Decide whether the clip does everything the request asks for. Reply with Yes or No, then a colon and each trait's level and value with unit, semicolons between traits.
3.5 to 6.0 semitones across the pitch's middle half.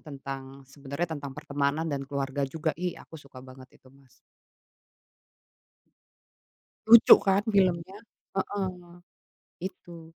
Yes: average, 4.3 semitones